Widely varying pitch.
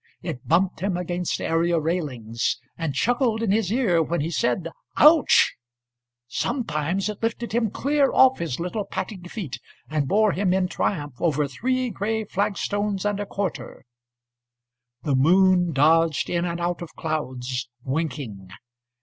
Yes: wide, 7.6 semitones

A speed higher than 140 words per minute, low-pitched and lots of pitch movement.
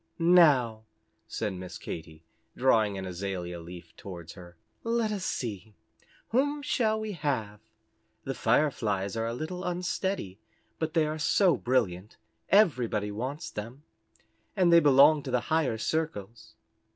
No: slow, 135 wpm; low, 125 Hz; wide, 8.8 semitones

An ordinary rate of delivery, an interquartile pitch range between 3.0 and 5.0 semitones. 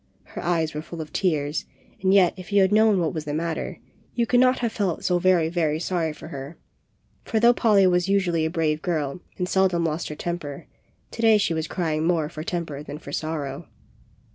No: fast, 215 wpm; average, 3.4 semitones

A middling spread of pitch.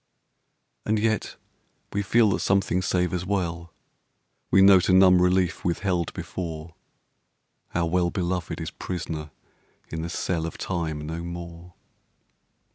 No: narrow, 1.8 semitones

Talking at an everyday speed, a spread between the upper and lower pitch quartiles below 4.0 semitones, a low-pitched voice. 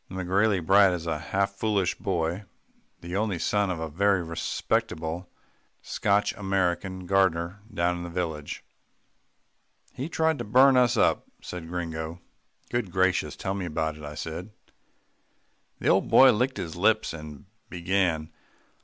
Yes: average, 145 wpm; average, 3.3 semitones; very low, 90 Hz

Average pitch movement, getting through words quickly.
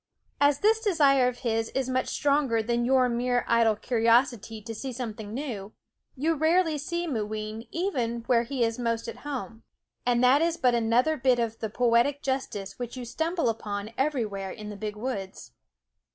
No: average, 3.5 semitones; average, 175 wpm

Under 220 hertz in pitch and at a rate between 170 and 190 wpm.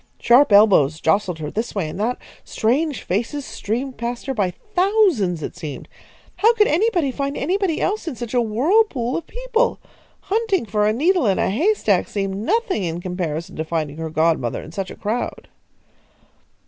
No: high, 230 Hz; average, 175 wpm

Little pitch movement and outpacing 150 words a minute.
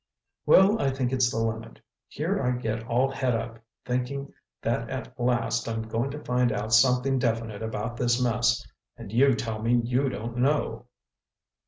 Yes: narrow, 2.0 semitones; average, 165 wpm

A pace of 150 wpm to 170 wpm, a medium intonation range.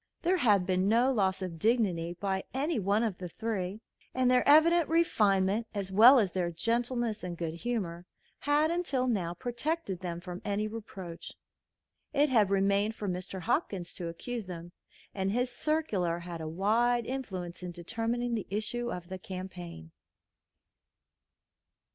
Yes: average, 155 wpm; average, 5.0 semitones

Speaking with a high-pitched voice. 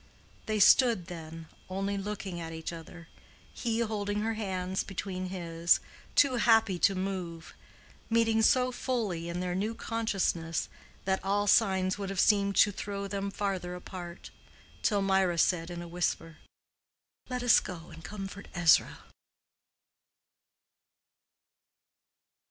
Yes: high, 195 Hz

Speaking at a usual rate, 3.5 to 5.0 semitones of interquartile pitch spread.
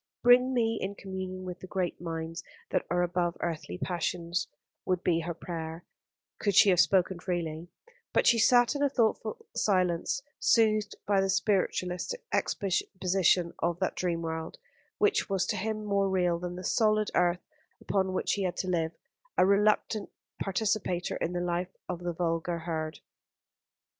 No: average, 160 wpm; average, 2.7 semitones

